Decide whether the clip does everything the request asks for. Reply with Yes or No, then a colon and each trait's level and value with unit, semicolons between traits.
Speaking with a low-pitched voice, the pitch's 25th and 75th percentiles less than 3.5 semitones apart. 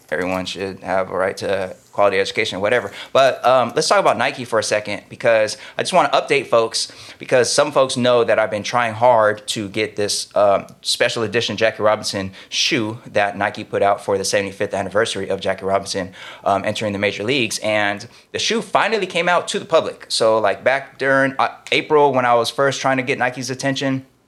No: low, 115 Hz; average, 4.3 semitones